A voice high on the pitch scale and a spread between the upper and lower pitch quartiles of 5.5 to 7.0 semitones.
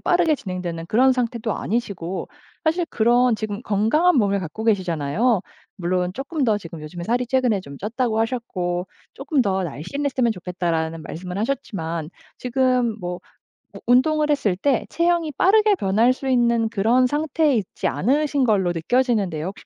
Yes: high, 225 Hz; wide, 6.2 semitones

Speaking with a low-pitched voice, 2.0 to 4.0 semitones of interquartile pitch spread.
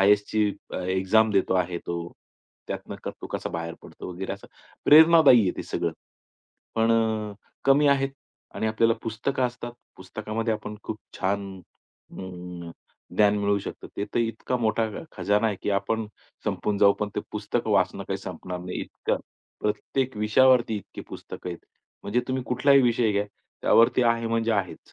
Yes: low, 110 Hz; average, 2.9 semitones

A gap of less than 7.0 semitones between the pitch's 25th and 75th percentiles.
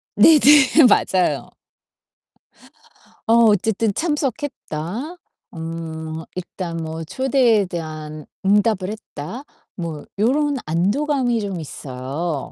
No: wide, 7.9 semitones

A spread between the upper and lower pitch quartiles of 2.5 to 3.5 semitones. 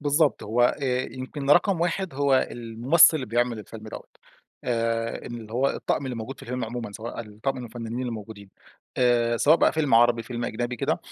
Yes: average, 2.9 semitones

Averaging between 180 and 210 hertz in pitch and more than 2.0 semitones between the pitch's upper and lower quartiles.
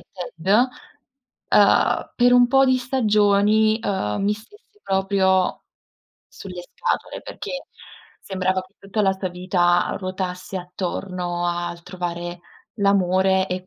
Yes: high, 190 Hz; narrow, 2.5 semitones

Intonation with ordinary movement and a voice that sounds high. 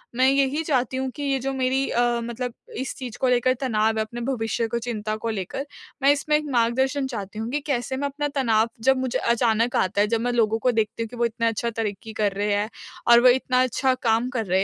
Yes: average, 3.0 semitones; high, 240 Hz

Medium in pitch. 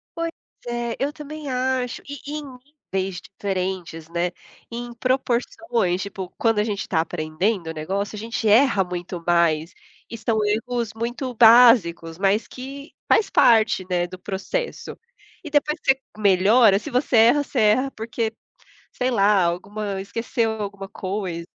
No: high, 215 Hz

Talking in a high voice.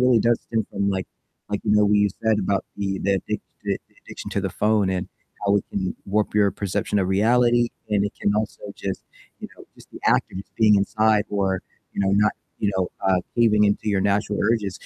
No: low, 105 Hz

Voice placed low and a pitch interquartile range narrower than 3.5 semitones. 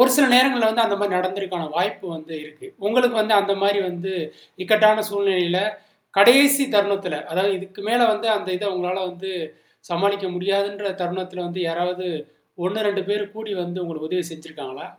No: high, 195 Hz; average, 2.8 semitones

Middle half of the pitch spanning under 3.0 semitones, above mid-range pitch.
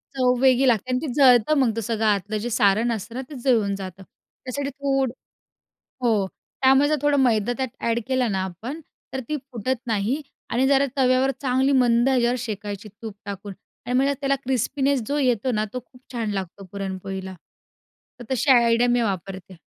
No: average, 4.1 semitones; high, 240 Hz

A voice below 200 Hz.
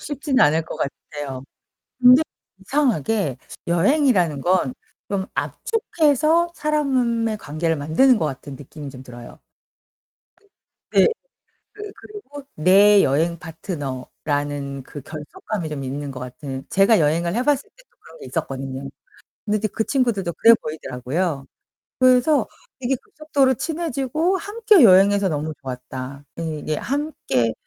Yes: medium, 185 Hz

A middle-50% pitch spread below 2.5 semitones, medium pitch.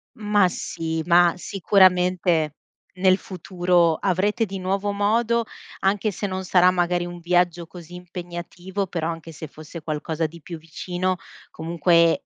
Yes: narrow, 2.1 semitones; medium, 180 Hz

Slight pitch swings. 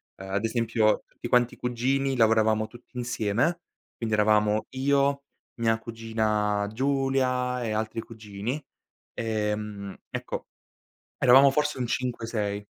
No: average, 3.0 semitones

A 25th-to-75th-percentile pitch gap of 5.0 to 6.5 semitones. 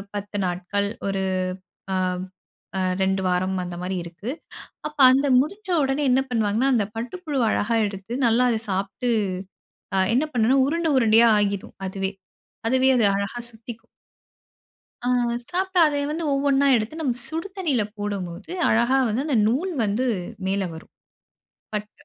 Yes: average, 5.3 semitones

